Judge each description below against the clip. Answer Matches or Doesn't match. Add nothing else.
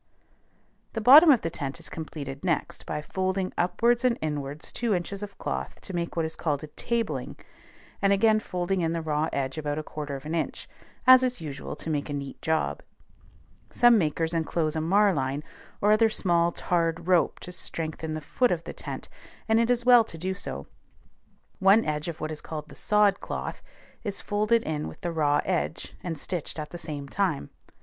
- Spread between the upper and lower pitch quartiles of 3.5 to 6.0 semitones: Matches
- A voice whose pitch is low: Doesn't match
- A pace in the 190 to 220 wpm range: Matches